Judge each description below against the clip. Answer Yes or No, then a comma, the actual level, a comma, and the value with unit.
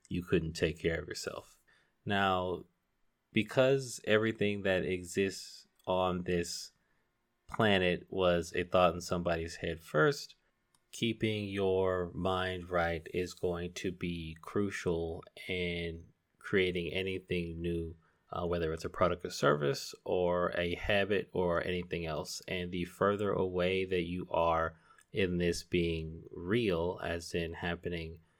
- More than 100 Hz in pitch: No, very low, 90 Hz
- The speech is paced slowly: Yes, slow, 130 wpm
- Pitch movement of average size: No, narrow, 1.8 semitones